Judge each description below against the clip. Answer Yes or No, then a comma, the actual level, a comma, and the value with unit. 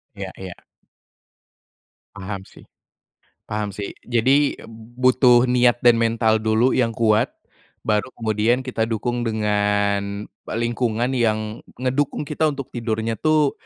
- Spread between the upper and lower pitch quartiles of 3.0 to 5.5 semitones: No, narrow, 2.6 semitones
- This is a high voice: No, low, 115 Hz